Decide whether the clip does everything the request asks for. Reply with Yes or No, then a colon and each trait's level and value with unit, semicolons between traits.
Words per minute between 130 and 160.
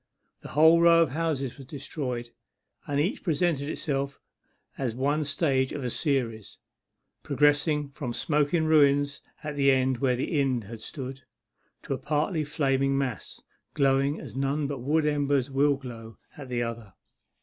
Yes: average, 155 wpm